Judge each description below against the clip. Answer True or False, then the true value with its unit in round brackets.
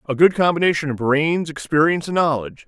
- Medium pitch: True (150 Hz)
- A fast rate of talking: False (180 wpm)